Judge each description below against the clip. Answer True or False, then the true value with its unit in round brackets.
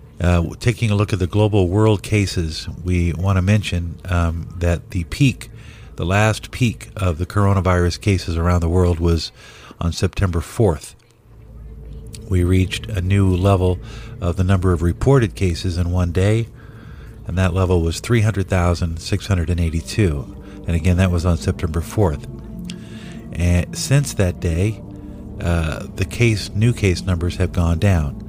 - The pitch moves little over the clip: False (3.5 semitones)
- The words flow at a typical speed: True (165 wpm)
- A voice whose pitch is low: True (95 Hz)